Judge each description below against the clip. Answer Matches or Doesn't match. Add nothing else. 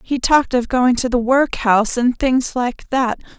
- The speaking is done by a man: Doesn't match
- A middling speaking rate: Matches